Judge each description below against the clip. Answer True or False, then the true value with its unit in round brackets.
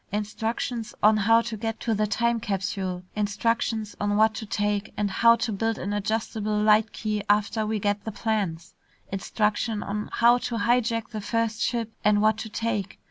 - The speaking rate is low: False (180 wpm)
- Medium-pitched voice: False (215 Hz)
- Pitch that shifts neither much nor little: False (1.6 semitones)